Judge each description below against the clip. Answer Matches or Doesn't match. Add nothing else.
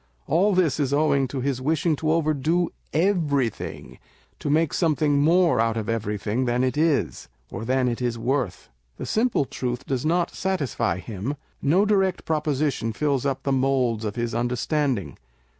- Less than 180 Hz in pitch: Matches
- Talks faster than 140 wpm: Matches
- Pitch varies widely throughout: Doesn't match